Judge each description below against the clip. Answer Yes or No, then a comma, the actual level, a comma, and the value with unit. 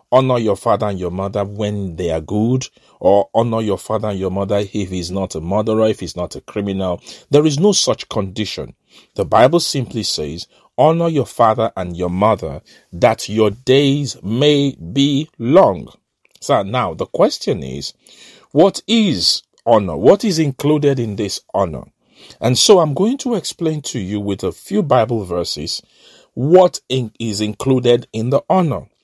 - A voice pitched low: Yes, low, 110 Hz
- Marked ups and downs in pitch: Yes, wide, 5.9 semitones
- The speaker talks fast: No, average, 170 wpm